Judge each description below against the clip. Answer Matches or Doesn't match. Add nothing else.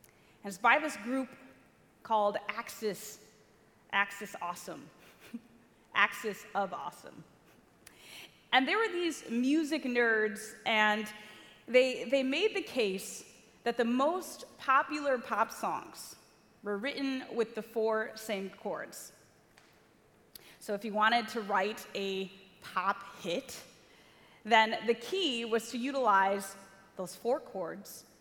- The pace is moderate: Doesn't match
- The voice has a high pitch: Matches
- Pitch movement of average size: Matches